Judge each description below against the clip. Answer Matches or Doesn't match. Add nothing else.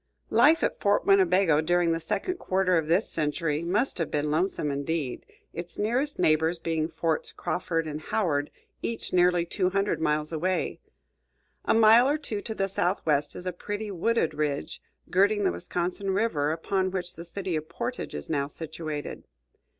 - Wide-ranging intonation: Doesn't match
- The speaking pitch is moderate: Matches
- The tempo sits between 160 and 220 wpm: Matches